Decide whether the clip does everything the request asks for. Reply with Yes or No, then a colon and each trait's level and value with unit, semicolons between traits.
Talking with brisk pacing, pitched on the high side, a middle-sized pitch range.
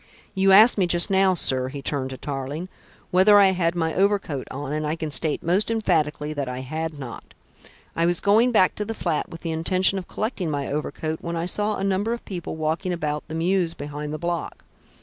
No: fast, 215 wpm; medium, 170 Hz; average, 4.2 semitones